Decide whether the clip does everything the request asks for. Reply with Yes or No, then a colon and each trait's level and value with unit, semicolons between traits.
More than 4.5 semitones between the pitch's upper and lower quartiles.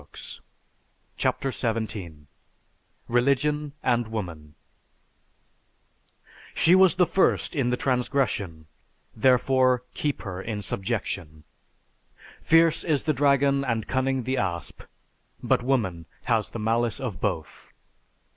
Yes: average, 5.0 semitones